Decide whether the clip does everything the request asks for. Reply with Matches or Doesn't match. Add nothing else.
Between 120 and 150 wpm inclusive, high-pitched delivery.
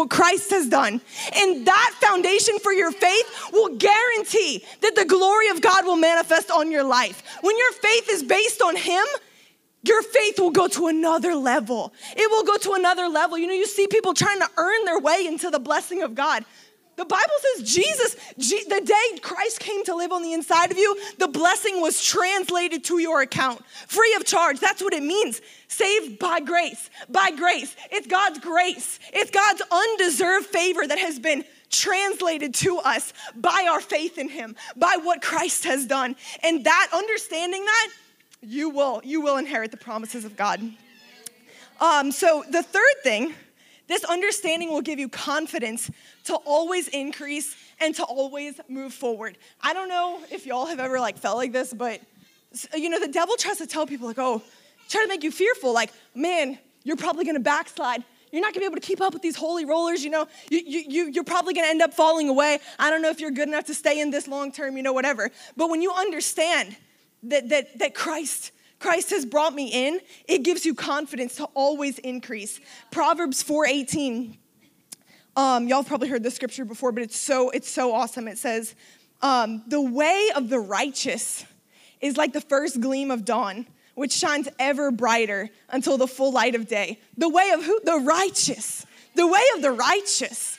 Doesn't match